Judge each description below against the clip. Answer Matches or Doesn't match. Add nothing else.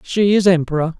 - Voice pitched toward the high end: Doesn't match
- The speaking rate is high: Doesn't match